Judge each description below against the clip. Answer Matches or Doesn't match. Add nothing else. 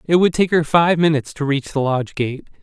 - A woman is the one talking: Doesn't match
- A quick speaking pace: Matches